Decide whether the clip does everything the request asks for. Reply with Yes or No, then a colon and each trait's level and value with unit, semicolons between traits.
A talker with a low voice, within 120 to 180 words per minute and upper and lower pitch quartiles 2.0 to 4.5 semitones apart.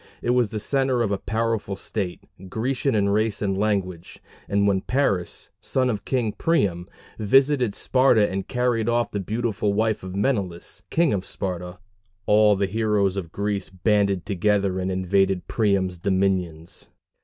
Yes: low, 100 Hz; average, 155 wpm; average, 3.0 semitones